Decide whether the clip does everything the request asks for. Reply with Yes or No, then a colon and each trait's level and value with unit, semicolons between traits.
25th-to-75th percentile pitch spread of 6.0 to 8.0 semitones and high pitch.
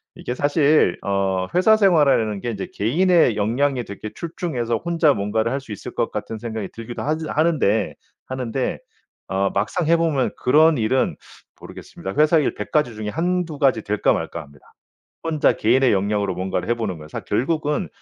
No: wide, 6.9 semitones; low, 125 Hz